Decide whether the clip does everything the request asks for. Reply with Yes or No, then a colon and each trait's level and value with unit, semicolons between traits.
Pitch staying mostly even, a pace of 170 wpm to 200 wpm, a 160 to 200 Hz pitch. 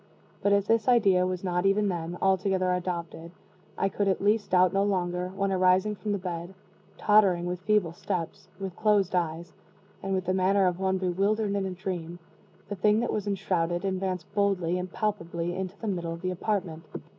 Yes: narrow, 2.1 semitones; average, 190 wpm; medium, 185 Hz